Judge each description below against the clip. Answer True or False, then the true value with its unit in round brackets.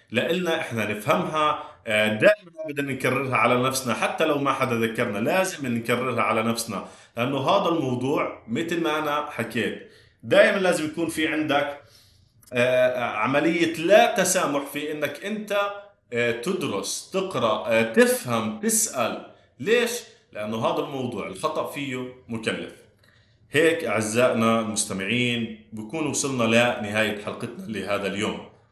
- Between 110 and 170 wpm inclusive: True (115 wpm)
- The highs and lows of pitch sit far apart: True (6.1 semitones)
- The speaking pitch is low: True (130 Hz)